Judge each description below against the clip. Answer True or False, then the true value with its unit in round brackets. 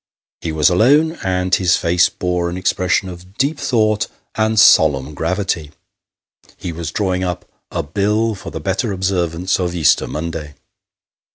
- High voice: False (90 Hz)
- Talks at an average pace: True (155 wpm)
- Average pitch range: True (3.4 semitones)